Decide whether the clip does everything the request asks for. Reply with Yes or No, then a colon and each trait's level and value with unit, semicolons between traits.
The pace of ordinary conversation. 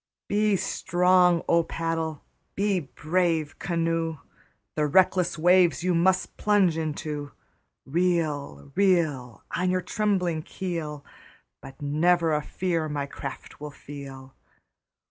No: slow, 110 wpm